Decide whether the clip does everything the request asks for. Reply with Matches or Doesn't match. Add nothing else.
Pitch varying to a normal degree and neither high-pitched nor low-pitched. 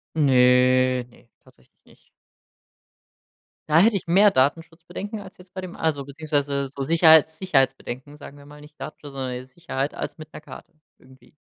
Matches